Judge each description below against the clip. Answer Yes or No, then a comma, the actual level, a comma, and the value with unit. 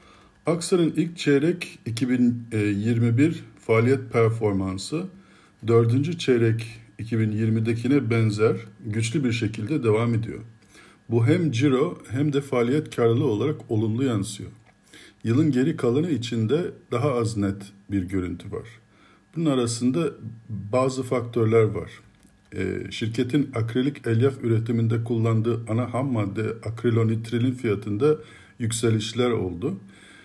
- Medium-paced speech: Yes, average, 105 wpm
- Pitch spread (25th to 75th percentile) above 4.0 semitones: No, average, 3.4 semitones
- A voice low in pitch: Yes, low, 115 Hz